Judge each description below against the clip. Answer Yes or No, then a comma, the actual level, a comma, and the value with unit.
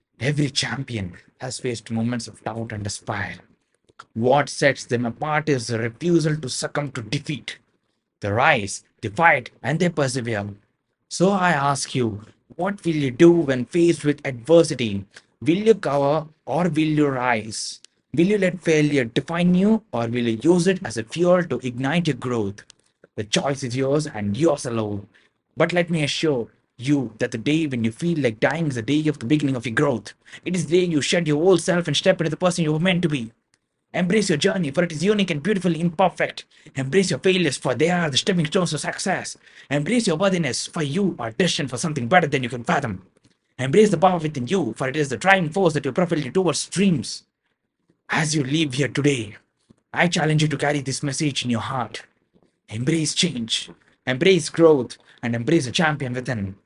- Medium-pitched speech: Yes, medium, 150 Hz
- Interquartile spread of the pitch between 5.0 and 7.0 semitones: Yes, wide, 5.6 semitones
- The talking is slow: No, average, 200 wpm